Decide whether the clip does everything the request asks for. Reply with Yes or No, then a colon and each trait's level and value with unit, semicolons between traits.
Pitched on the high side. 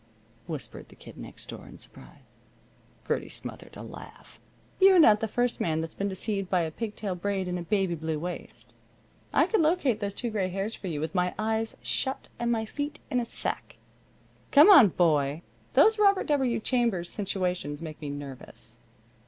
Yes: high, 200 Hz